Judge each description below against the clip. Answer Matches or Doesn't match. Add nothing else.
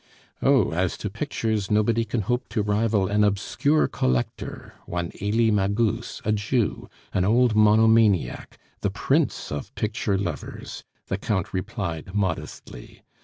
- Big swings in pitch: Doesn't match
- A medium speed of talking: Doesn't match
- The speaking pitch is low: Matches